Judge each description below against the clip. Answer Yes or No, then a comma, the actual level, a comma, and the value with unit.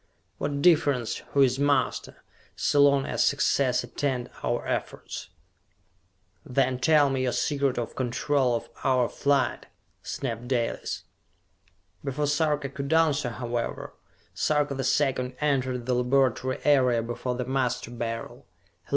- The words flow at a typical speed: No, slow, 125 wpm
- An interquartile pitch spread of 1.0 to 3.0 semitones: Yes, narrow, 2.4 semitones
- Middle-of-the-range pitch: No, low, 130 Hz